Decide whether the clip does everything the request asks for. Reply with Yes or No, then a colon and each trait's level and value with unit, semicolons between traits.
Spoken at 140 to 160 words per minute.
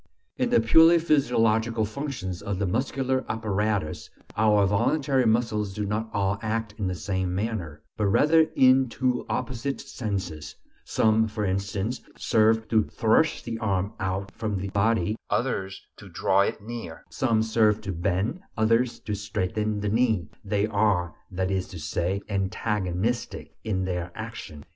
Yes: average, 150 wpm